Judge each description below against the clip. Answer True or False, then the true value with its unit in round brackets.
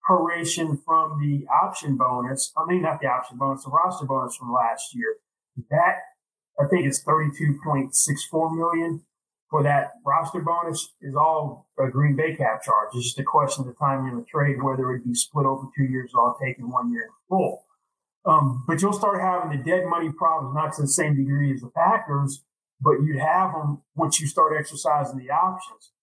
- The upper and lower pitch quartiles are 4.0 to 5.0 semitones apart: False (3.5 semitones)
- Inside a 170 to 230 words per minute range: True (205 wpm)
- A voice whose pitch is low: False (150 Hz)